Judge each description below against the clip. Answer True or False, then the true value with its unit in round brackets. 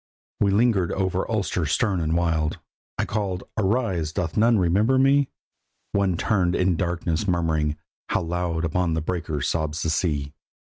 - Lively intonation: False (3.6 semitones)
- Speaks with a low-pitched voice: True (90 Hz)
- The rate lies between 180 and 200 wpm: False (155 wpm)